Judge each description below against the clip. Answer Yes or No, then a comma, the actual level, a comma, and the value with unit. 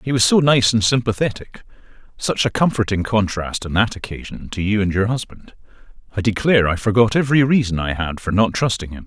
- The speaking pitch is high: No, low, 105 Hz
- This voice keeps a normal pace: Yes, average, 185 wpm